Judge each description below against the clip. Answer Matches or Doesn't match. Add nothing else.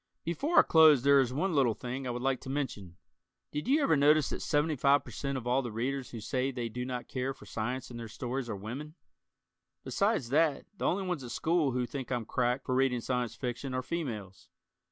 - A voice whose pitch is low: Matches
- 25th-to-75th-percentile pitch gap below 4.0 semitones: Matches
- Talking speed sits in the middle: Doesn't match